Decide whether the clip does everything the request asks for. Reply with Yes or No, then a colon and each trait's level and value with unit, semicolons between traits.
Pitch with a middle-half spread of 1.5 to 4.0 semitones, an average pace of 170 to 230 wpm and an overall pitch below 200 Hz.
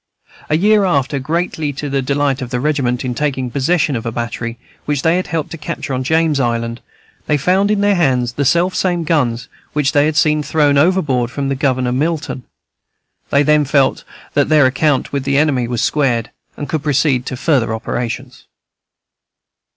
Yes: average, 3.5 semitones; average, 180 wpm; medium, 140 Hz